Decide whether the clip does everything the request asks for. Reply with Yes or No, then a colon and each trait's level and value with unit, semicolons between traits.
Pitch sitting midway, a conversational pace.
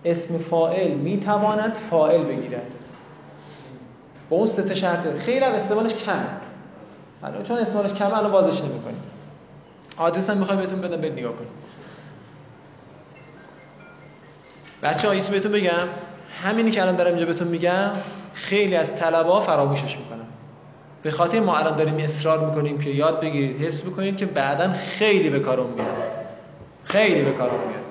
Yes: medium, 175 Hz; average, 145 wpm